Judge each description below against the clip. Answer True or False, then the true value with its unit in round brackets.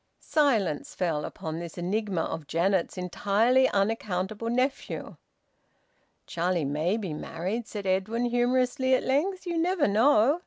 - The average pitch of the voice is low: False (210 Hz)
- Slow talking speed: True (125 wpm)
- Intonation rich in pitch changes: True (6.1 semitones)